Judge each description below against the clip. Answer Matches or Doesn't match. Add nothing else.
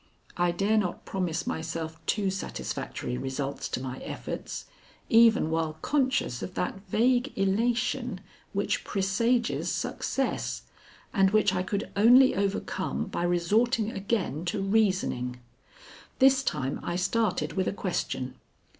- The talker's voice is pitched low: Doesn't match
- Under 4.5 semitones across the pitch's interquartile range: Doesn't match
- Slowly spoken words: Matches